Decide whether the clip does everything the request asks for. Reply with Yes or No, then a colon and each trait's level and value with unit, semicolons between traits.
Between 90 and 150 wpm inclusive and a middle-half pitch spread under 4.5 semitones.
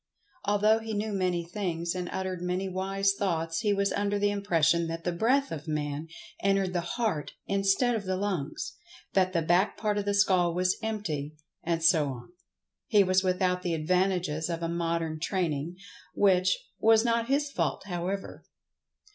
No: average, 165 wpm; average, 3.3 semitones